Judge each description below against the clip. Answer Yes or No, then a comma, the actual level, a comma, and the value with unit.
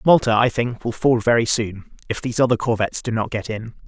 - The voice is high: No, low, 115 Hz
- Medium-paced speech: No, fast, 230 wpm